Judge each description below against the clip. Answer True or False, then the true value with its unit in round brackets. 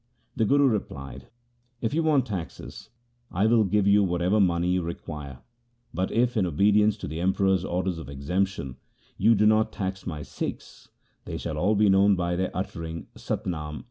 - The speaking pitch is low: True (95 Hz)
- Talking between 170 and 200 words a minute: True (180 wpm)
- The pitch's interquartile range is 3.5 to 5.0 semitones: True (3.8 semitones)